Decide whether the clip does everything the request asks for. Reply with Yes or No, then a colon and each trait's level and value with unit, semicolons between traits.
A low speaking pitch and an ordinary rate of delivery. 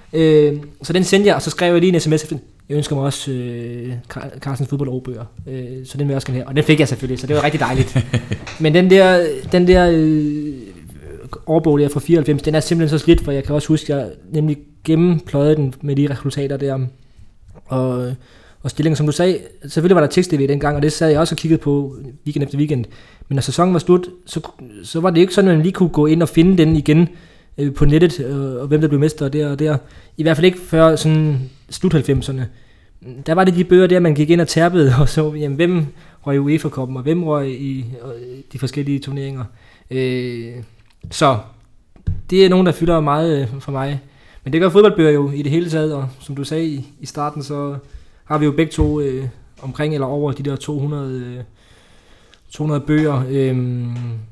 No: medium, 145 Hz; average, 215 wpm